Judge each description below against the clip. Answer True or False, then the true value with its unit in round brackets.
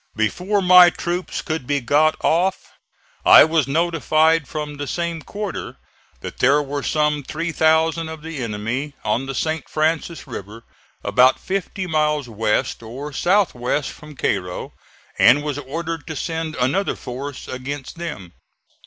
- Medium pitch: True (150 Hz)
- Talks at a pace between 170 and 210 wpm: False (145 wpm)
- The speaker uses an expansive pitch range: False (3.8 semitones)